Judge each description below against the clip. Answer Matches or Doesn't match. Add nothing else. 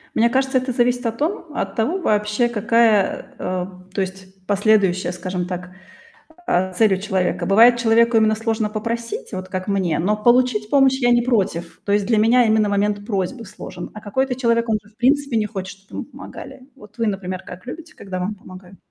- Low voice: Doesn't match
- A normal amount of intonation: Matches